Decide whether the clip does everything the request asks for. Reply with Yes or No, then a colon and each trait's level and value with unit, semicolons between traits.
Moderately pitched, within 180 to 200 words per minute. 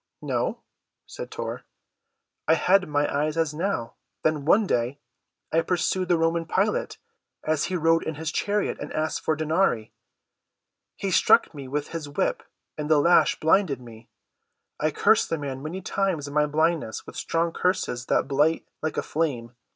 No: medium, 155 Hz; average, 165 wpm